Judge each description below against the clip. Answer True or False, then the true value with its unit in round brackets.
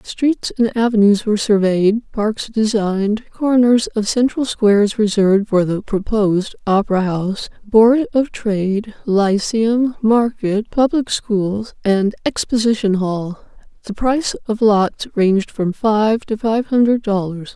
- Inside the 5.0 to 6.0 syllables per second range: False (4.1 syllables/s)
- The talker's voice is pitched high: True (215 Hz)